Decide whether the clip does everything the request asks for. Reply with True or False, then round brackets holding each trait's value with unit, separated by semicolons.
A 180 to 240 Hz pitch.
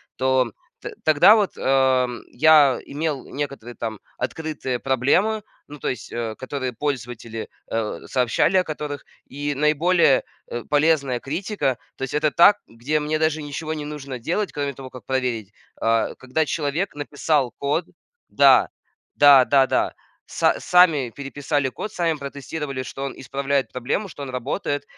False (140 Hz)